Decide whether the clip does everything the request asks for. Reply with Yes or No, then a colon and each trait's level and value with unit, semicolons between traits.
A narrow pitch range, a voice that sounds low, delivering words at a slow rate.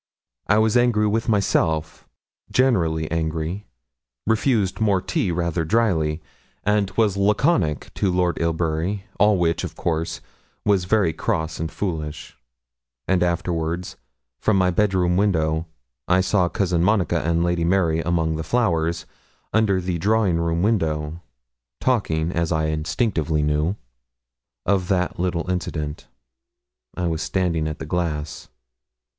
No: average, 3.8 semitones; very low, 85 Hz; slow, 130 wpm